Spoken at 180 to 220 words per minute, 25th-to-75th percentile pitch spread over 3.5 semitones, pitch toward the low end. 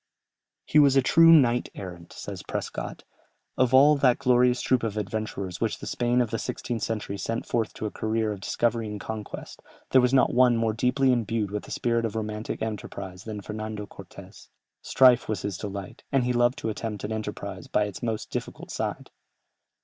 No: average, 190 wpm; average, 2.8 semitones; low, 115 Hz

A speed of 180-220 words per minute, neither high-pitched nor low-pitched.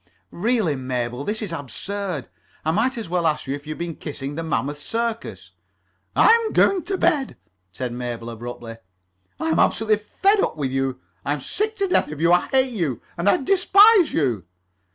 Yes: average, 185 wpm; medium, 165 Hz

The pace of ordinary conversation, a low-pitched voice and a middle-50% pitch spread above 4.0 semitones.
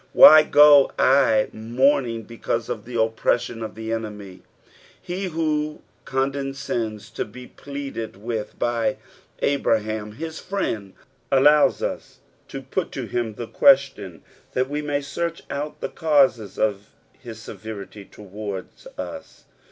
No: slow, 130 wpm; low, 120 Hz; average, 4.7 semitones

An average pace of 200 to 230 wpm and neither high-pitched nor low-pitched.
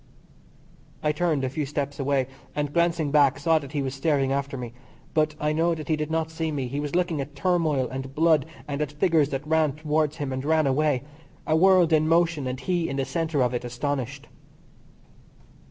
Yes: fast, 205 wpm; medium, 150 Hz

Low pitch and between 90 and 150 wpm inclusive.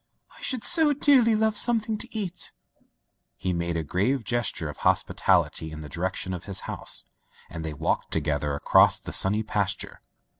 No: low, 100 Hz; average, 175 wpm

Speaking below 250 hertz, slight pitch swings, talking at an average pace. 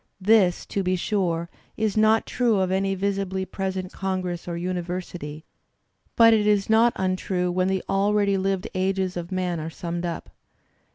Yes: high, 190 Hz; narrow, 1.8 semitones; average, 160 wpm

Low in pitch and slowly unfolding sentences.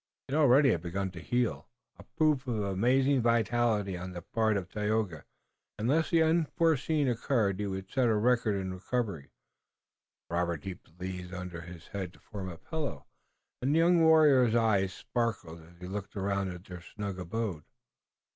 No: low, 105 Hz; average, 175 wpm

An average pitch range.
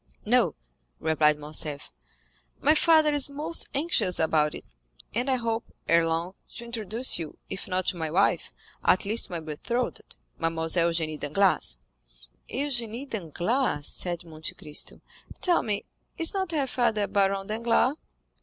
No: wide, 7.3 semitones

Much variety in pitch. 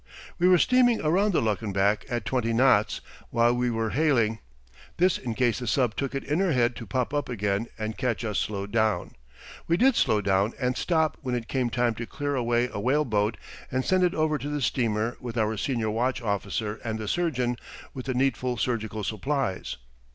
No: average, 3.9 semitones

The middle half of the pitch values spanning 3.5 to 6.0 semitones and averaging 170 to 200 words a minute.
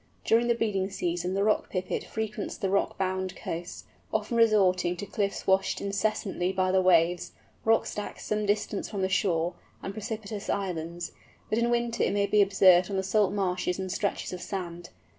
No: narrow, 2.4 semitones; average, 180 wpm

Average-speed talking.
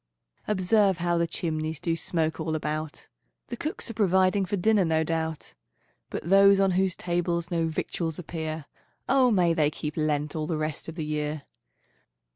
Yes: average, 170 wpm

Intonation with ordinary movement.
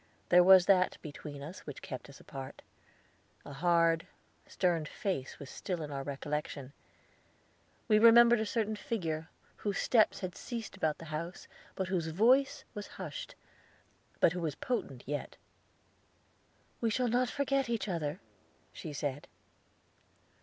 No: wide, 6.4 semitones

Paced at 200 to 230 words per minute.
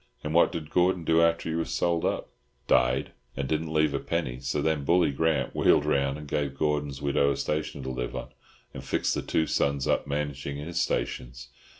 Yes: fast, 205 wpm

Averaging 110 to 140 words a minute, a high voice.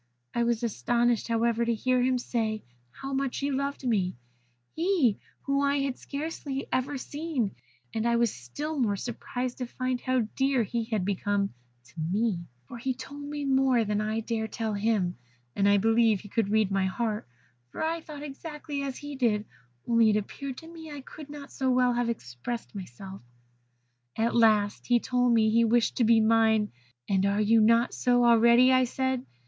No: average, 190 wpm; high, 235 Hz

